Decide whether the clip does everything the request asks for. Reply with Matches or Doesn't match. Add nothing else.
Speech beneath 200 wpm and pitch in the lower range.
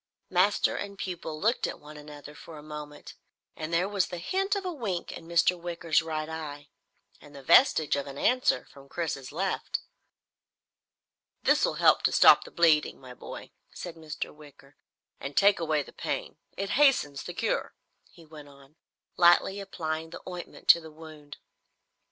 Doesn't match